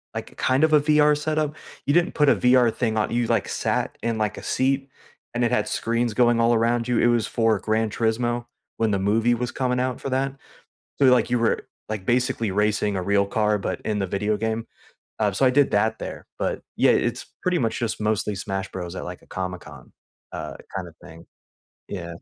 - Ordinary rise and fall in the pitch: Yes, average, 3.2 semitones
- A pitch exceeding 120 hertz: No, low, 115 Hz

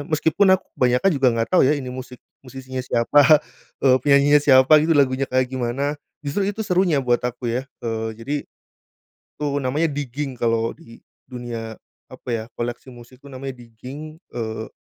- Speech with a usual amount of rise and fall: Yes, average, 3.2 semitones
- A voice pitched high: No, low, 130 Hz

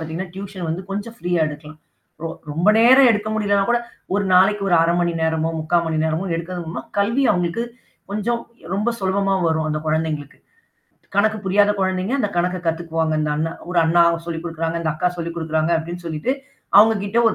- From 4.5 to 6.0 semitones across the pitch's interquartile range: No, average, 3.9 semitones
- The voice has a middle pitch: Yes, medium, 175 Hz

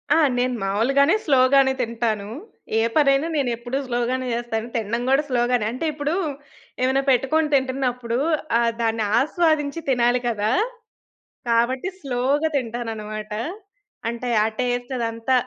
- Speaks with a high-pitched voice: Yes, high, 245 Hz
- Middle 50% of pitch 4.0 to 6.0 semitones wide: No, average, 2.8 semitones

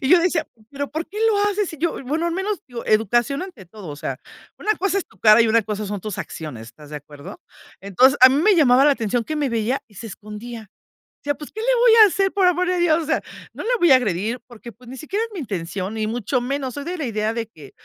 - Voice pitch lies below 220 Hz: No, very high, 255 Hz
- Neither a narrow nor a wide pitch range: No, wide, 7.7 semitones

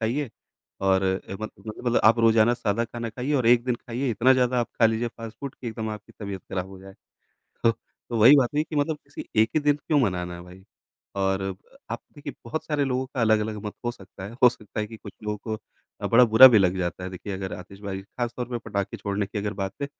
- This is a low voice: Yes, low, 110 Hz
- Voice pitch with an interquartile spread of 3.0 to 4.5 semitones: Yes, average, 3.9 semitones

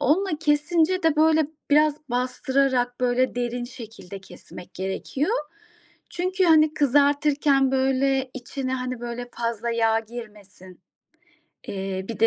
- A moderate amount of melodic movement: Yes, average, 4.0 semitones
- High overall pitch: Yes, very high, 260 Hz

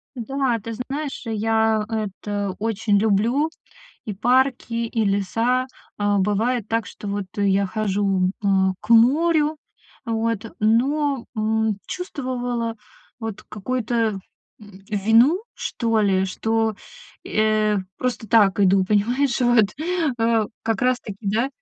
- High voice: Yes, high, 225 Hz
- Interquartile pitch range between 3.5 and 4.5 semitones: No, average, 2.9 semitones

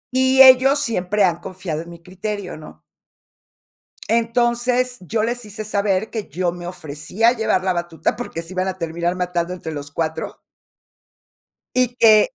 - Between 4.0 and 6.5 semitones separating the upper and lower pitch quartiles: Yes, average, 5.1 semitones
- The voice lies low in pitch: No, high, 190 Hz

